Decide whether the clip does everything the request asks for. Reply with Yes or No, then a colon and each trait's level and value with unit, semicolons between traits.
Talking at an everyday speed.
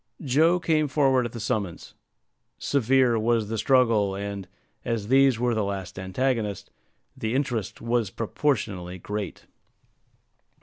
No: slow, 125 wpm